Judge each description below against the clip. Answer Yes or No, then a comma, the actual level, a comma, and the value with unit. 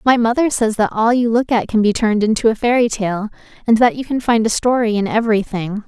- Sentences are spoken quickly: Yes, fast, 245 wpm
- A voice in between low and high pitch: No, high, 225 Hz